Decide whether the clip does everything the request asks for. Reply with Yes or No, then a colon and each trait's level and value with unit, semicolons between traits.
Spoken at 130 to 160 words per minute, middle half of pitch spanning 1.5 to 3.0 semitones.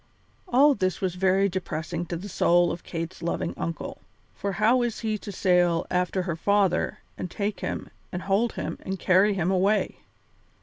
No: average, 175 wpm; narrow, 2.6 semitones